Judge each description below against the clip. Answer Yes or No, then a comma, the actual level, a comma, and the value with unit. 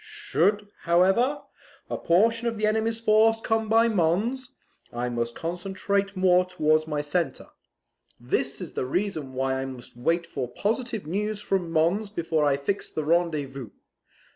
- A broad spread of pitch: Yes, wide, 6.1 semitones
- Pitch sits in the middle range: Yes, medium, 180 Hz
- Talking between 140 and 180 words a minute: Yes, average, 150 wpm